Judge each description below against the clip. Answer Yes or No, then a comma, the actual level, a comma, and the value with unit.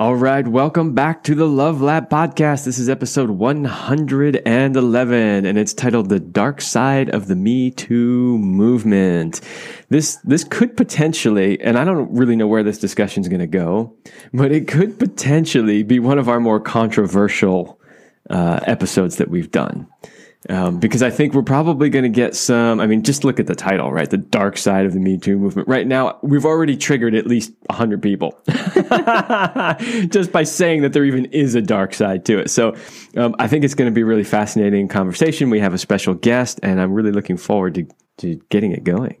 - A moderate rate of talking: Yes, average, 195 wpm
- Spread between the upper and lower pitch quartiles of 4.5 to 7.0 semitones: Yes, wide, 5.4 semitones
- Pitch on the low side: Yes, low, 125 Hz